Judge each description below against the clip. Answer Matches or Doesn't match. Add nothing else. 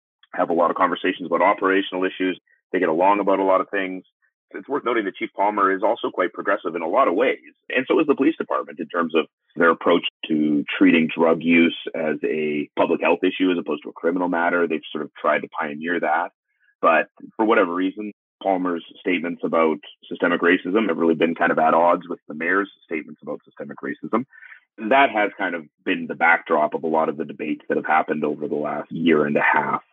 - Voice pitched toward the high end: Doesn't match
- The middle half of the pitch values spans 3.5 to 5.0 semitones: Matches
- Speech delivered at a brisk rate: Matches